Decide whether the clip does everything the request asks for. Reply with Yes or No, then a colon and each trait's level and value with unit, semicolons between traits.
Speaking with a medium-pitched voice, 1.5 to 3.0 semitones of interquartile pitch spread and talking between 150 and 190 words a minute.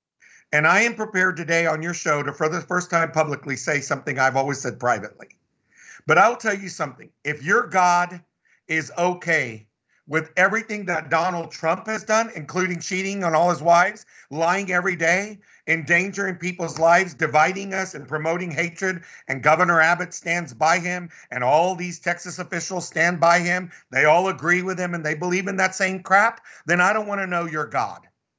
Yes: medium, 175 Hz; narrow, 2.6 semitones; average, 185 wpm